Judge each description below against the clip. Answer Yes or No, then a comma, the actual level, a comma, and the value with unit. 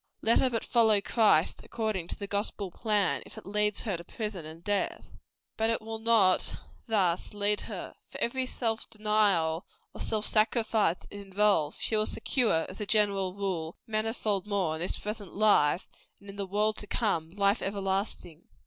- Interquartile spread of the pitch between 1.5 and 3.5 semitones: Yes, narrow, 2.5 semitones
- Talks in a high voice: Yes, high, 205 Hz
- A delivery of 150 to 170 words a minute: No, average, 180 wpm